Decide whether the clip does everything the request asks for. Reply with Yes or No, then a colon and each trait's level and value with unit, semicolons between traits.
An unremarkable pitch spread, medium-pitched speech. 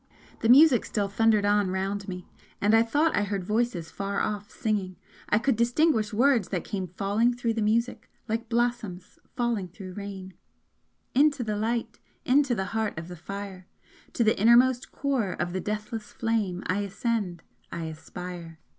No: average, 3.7 semitones; high, 210 Hz